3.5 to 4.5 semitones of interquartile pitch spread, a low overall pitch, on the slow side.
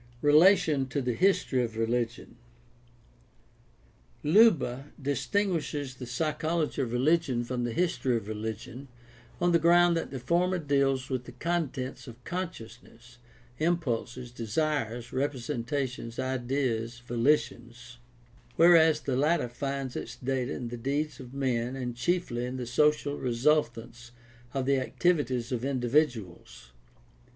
Yes: average, 3.9 semitones; low, 130 Hz; slow, 125 wpm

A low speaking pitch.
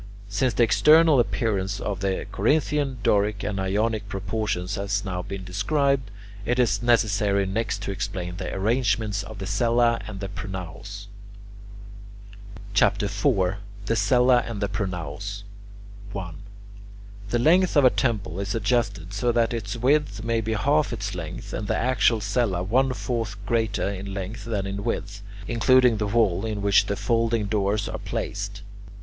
Yes: low, 105 Hz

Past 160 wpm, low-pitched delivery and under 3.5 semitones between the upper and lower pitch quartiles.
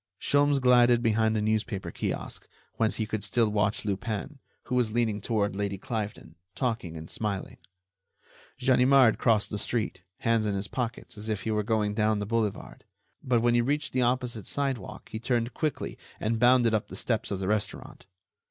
Yes: average, 180 wpm; low, 110 Hz; narrow, 2.6 semitones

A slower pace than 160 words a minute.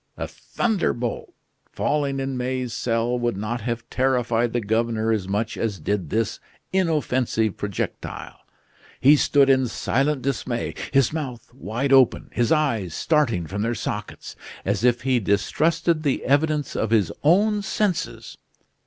Yes: average, 140 wpm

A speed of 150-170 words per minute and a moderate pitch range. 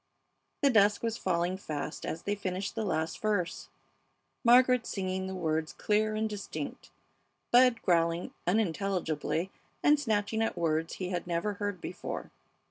No: average, 140 wpm; average, 4.0 semitones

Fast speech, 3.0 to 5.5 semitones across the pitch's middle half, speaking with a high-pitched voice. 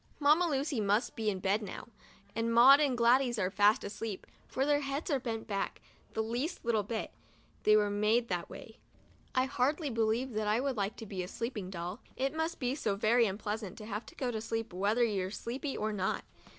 Yes: fast, 215 wpm; average, 3.8 semitones; high, 225 Hz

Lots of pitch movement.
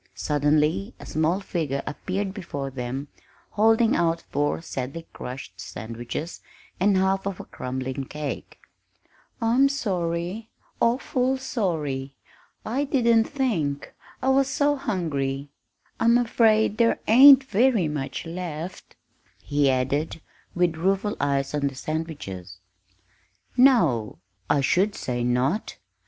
Yes: wide, 8.1 semitones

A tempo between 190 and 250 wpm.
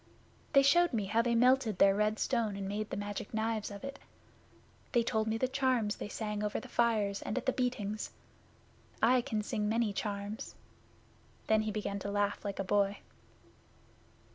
No: average, 180 wpm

